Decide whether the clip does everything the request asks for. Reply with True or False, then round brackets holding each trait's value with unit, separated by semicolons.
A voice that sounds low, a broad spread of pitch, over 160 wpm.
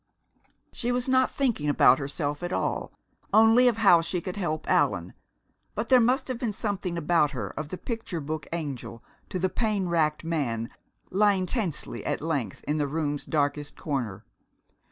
False (170 Hz; 6.3 semitones; 170 wpm)